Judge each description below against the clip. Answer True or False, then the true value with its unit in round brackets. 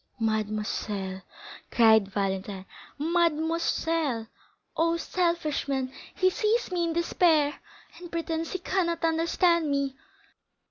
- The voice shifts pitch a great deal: True (7.2 semitones)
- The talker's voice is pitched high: True (320 Hz)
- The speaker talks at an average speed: False (100 wpm)